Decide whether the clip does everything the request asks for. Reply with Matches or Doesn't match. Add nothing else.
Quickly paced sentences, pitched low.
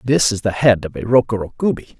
Matches